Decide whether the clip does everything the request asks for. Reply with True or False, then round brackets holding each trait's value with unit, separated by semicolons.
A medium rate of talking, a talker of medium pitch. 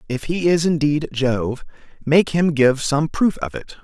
True (190 wpm; 145 Hz)